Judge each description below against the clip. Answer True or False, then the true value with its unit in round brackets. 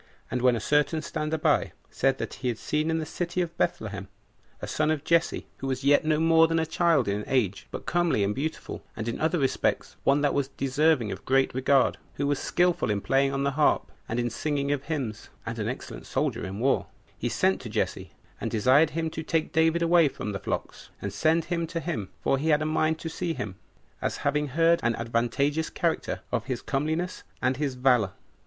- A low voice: False (145 Hz)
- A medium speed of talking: False (215 wpm)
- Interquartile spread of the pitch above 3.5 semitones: True (4.3 semitones)